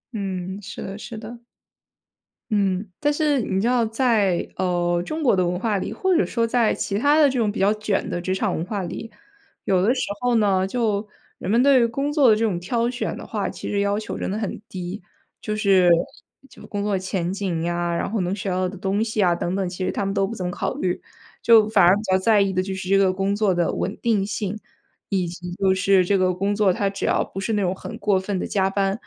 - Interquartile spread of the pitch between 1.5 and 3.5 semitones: Yes, average, 2.9 semitones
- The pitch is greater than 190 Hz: Yes, high, 200 Hz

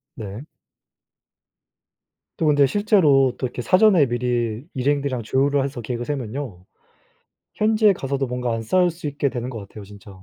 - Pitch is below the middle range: Yes, low, 130 Hz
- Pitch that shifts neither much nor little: Yes, average, 3.7 semitones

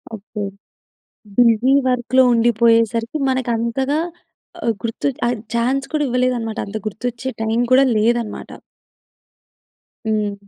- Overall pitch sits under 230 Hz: No, high, 235 Hz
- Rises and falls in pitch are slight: Yes, narrow, 2.1 semitones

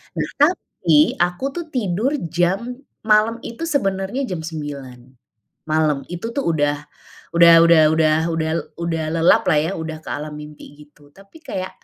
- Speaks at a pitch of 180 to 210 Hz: No, medium, 170 Hz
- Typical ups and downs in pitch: No, wide, 6.1 semitones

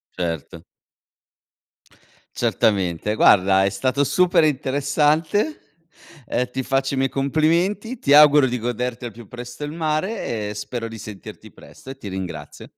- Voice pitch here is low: Yes, low, 130 Hz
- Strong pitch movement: Yes, wide, 5.9 semitones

